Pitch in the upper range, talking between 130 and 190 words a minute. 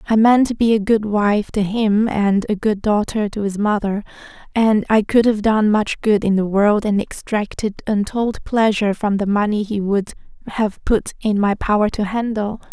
No: high, 210 Hz; average, 200 wpm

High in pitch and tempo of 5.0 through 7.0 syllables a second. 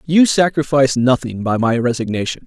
No: low, 130 Hz; 5.5 syllables/s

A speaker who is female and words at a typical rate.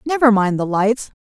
Yes: female; average, 195 wpm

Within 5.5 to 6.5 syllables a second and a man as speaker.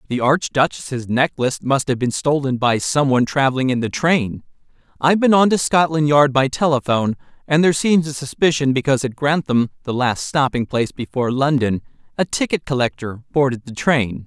Yes: 5.6 syllables/s; male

